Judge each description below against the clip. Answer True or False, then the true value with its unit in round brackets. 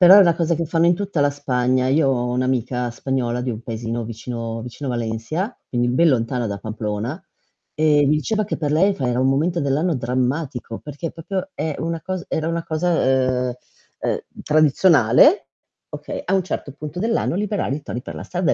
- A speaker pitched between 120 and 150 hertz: True (140 Hz)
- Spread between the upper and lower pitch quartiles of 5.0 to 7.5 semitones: True (5.4 semitones)